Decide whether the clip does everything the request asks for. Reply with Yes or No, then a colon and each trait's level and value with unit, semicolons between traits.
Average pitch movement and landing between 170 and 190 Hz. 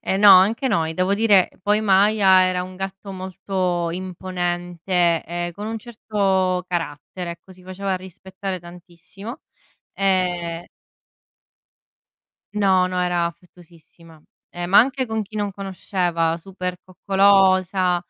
No: narrow, 2.0 semitones; medium, 185 Hz